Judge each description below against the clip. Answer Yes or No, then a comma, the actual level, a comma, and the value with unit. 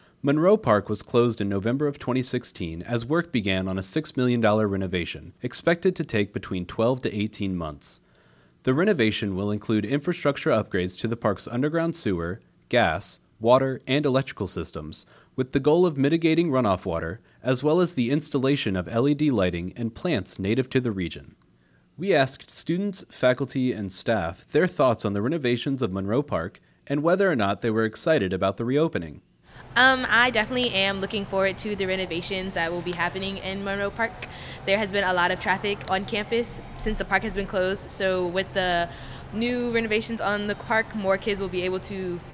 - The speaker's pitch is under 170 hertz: Yes, medium, 140 Hz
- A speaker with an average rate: Yes, average, 185 wpm